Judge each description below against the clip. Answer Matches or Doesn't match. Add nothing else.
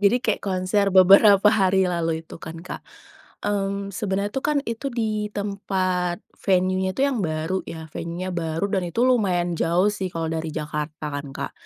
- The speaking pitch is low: Doesn't match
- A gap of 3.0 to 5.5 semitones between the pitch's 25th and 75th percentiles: Matches